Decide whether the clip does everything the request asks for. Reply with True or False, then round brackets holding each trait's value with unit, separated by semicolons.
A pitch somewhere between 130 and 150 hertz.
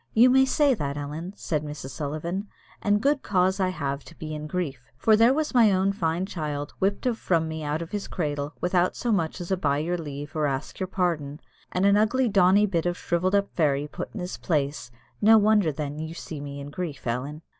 False (170 Hz)